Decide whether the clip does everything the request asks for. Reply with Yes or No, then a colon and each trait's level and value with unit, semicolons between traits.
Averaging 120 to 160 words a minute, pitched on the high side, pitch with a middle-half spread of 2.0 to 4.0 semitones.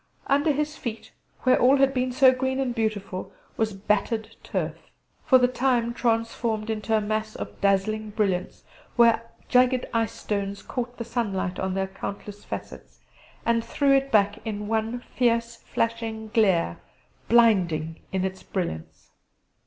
Yes: average, 145 wpm; high, 225 Hz; average, 3.3 semitones